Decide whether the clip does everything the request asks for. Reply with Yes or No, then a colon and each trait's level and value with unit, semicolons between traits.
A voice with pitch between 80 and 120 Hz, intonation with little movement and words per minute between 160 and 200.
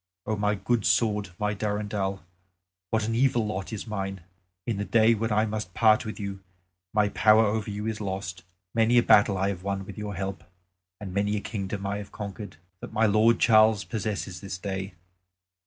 Yes: low, 105 Hz; narrow, 1.8 semitones; average, 190 wpm